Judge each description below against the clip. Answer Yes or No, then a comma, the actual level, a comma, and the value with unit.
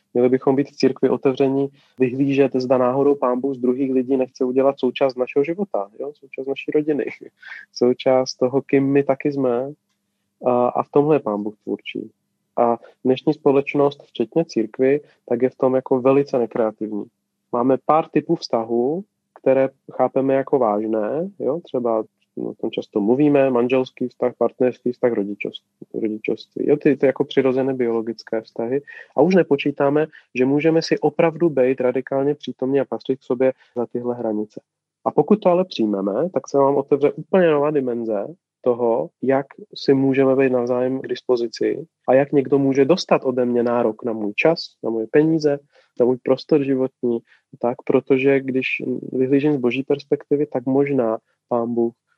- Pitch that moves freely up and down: No, narrow, 2.5 semitones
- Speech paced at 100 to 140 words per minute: No, average, 160 wpm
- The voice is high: No, low, 130 Hz